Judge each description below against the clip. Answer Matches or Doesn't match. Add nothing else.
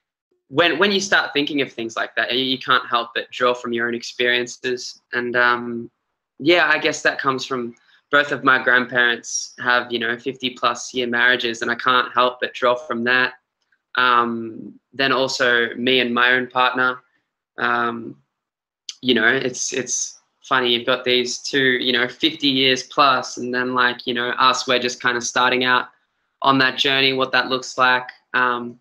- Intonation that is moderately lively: Doesn't match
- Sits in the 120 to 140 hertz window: Matches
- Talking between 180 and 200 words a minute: Matches